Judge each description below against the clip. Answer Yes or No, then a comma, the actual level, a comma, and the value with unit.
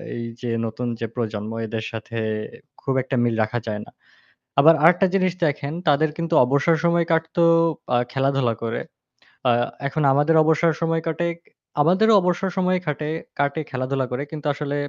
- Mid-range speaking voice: Yes, medium, 145 Hz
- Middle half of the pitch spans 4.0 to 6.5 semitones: Yes, average, 5.0 semitones